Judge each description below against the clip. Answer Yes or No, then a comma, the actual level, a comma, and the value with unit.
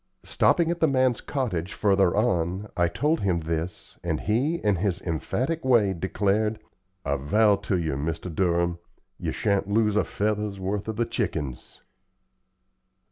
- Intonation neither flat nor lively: Yes, average, 4.3 semitones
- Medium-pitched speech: No, low, 100 Hz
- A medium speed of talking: Yes, average, 150 wpm